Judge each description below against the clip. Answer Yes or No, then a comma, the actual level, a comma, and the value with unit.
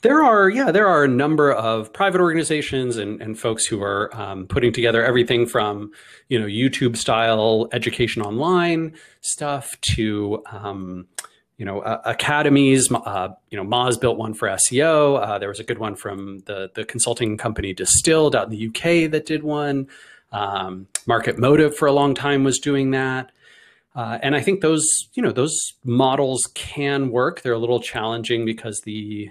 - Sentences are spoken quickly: No, average, 180 wpm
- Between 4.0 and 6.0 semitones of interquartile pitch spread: Yes, average, 4.3 semitones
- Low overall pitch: Yes, low, 120 Hz